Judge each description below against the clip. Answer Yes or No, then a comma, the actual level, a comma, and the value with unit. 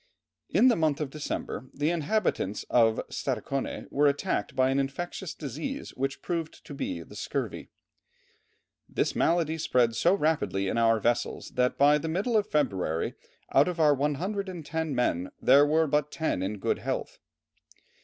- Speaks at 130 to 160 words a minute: Yes, average, 155 wpm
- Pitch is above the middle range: No, medium, 145 Hz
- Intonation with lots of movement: No, average, 4.4 semitones